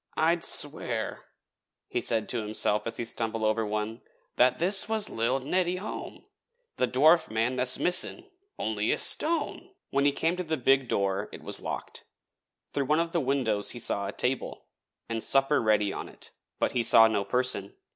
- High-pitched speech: No, low, 125 Hz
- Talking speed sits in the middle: Yes, average, 180 wpm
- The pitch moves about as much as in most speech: No, wide, 6.2 semitones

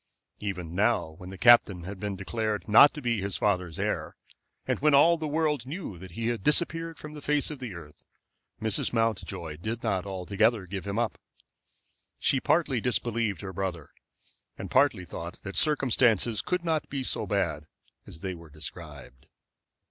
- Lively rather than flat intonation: Yes, wide, 6.2 semitones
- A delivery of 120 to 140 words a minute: No, average, 170 wpm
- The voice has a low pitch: Yes, low, 105 Hz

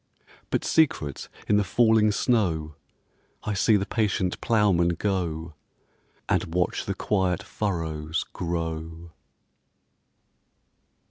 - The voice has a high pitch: No, very low, 90 Hz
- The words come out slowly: Yes, slow, 95 wpm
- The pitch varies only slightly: No, average, 4.3 semitones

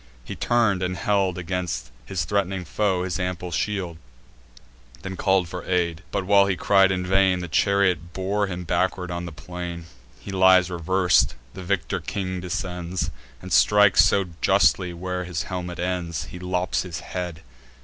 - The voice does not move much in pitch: Yes, narrow, 1.5 semitones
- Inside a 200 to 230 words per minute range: No, average, 160 wpm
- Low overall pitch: Yes, very low, 90 Hz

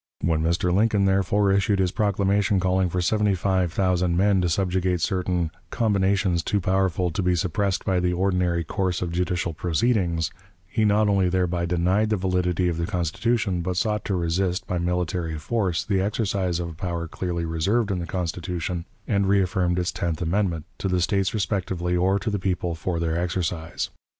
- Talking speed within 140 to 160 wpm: No, average, 180 wpm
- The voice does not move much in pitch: Yes, narrow, 2.2 semitones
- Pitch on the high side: No, very low, 90 Hz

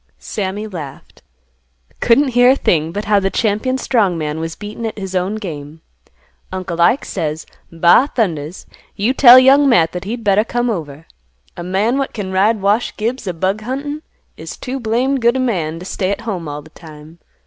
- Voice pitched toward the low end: No, high, 200 Hz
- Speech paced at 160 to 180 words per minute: No, average, 190 wpm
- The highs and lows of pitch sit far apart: Yes, wide, 5.9 semitones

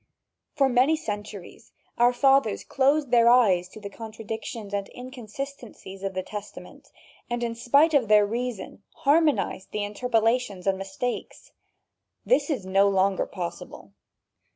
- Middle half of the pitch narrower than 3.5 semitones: No, average, 4.1 semitones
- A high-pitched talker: Yes, high, 225 Hz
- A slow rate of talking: Yes, slow, 130 wpm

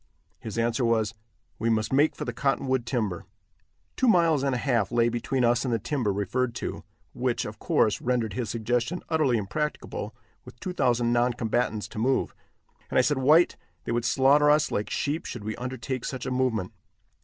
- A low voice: Yes, low, 120 Hz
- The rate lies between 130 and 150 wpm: No, average, 185 wpm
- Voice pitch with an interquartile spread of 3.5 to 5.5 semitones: No, average, 2.9 semitones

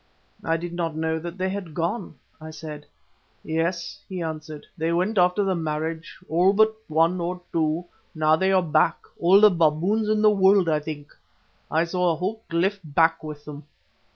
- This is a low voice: No, medium, 170 Hz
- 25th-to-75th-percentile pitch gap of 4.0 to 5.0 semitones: No, average, 2.9 semitones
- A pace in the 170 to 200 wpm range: Yes, average, 180 wpm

